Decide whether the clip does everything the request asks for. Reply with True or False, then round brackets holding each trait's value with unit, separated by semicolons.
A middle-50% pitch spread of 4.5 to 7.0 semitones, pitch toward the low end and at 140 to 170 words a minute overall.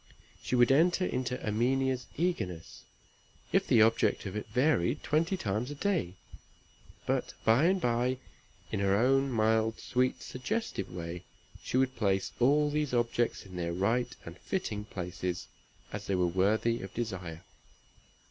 True (5.3 semitones; 115 Hz; 150 wpm)